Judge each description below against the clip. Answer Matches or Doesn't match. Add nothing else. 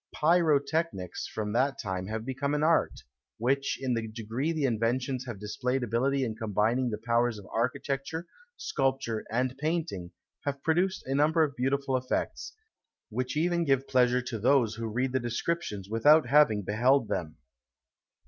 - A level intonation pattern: Doesn't match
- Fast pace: Doesn't match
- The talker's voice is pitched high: Doesn't match